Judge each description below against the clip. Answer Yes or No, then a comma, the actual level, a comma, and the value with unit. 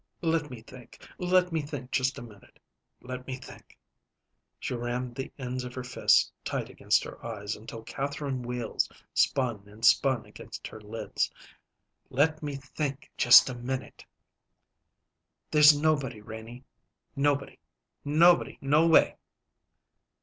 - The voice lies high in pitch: No, low, 130 Hz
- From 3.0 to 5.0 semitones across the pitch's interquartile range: Yes, average, 3.3 semitones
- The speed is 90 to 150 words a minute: Yes, slow, 135 wpm